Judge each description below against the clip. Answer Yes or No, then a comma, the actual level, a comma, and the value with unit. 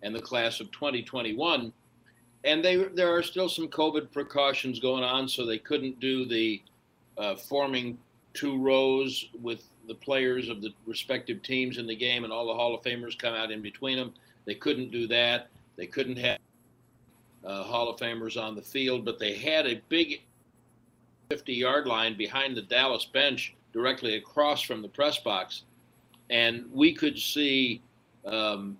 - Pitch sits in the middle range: No, low, 125 Hz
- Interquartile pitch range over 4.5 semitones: No, average, 2.8 semitones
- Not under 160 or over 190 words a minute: Yes, average, 170 wpm